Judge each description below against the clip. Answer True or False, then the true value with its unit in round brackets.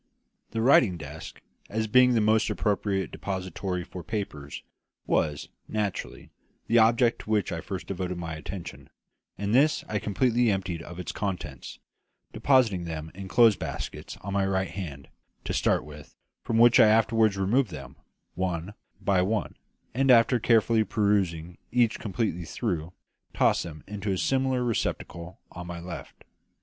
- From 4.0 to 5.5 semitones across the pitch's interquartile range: True (4.4 semitones)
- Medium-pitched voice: False (100 Hz)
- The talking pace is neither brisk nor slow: True (155 wpm)